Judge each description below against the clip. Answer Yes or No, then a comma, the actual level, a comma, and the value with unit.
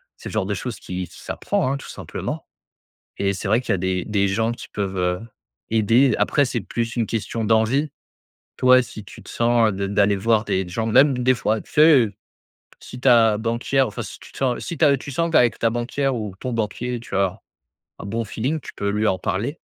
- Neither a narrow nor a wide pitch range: Yes, average, 3.7 semitones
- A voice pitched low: Yes, low, 115 Hz